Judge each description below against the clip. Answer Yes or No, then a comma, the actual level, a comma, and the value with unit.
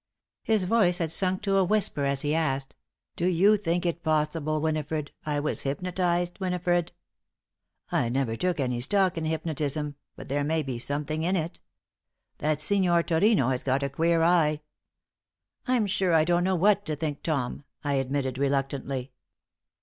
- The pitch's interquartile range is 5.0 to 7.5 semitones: No, average, 4.0 semitones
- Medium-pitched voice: Yes, medium, 160 Hz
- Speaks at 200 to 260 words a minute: No, average, 165 wpm